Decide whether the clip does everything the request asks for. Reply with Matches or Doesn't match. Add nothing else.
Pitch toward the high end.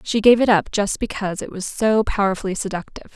Matches